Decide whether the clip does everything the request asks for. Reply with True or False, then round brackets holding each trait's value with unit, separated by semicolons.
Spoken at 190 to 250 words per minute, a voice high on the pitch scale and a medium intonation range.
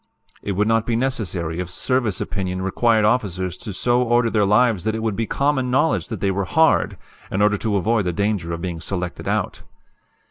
False (205 wpm; 105 Hz; 4.2 semitones)